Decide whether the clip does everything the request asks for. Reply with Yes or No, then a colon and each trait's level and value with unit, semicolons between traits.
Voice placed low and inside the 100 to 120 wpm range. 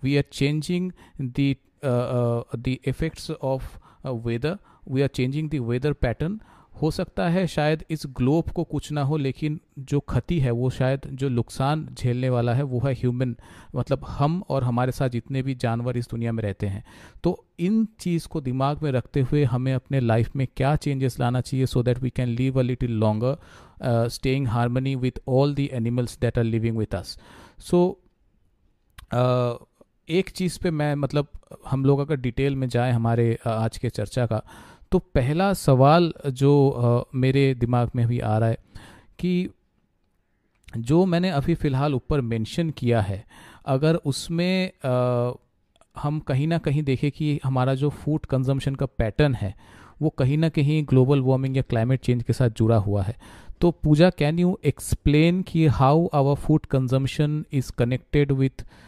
No: low, 130 Hz; average, 170 wpm